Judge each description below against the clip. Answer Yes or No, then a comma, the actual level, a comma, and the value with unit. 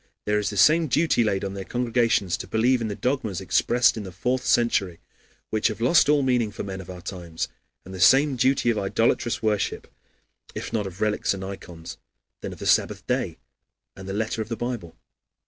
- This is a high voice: No, low, 110 Hz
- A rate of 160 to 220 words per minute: Yes, fast, 205 wpm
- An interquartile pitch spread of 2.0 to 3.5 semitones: No, average, 4.1 semitones